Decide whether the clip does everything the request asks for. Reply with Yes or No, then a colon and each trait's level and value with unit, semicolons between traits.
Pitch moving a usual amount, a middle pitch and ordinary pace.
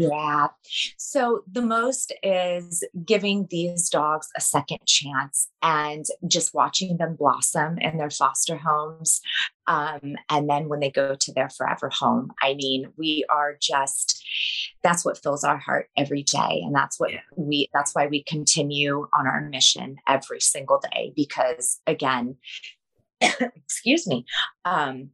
Yes: average, 3.4 semitones; medium, 150 Hz; average, 145 wpm